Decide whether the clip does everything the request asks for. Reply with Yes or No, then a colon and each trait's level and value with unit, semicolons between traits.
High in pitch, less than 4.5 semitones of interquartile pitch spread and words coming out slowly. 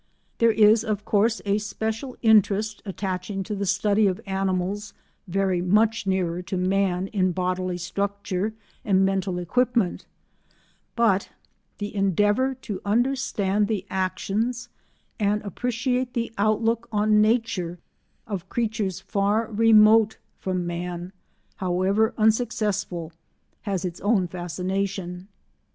Yes: high, 200 Hz; average, 2.8 semitones; slow, 115 wpm